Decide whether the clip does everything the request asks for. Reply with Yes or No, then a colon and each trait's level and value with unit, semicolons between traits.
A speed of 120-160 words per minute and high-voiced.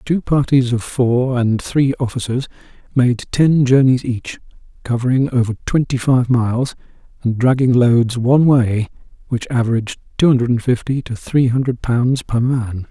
No: average, 150 wpm; low, 125 Hz